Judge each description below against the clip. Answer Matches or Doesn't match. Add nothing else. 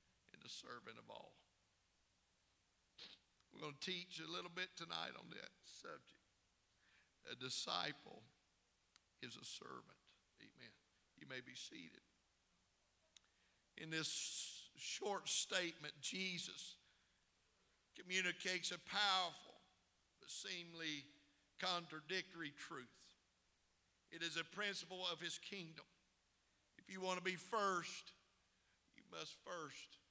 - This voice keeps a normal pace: Doesn't match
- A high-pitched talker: Doesn't match